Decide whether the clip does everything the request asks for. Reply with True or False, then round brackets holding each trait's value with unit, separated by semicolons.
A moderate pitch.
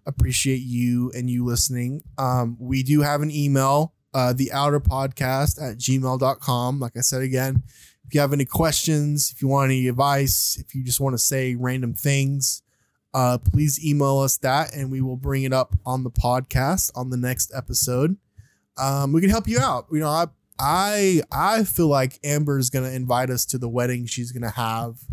False (130 Hz)